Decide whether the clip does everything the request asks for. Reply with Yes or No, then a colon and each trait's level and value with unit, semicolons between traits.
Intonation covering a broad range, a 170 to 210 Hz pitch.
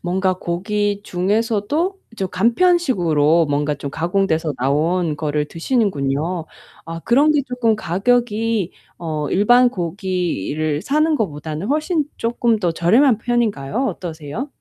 Yes: wide, 6.7 semitones; high, 190 Hz